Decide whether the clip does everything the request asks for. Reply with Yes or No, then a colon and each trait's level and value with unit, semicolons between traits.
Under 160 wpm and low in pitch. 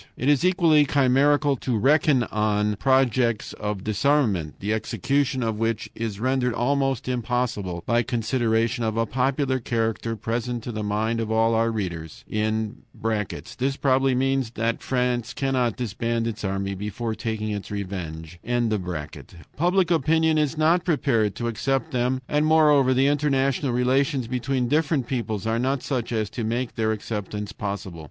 Yes: average, 150 wpm; low, 120 Hz